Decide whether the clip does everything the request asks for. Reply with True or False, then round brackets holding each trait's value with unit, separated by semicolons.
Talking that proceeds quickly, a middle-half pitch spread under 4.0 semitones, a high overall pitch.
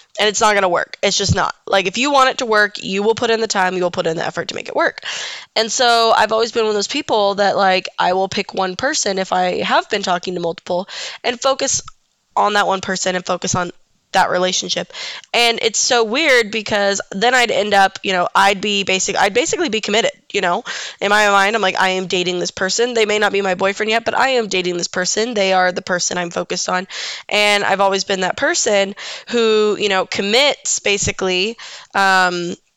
True (235 wpm; 3.2 semitones; 200 Hz)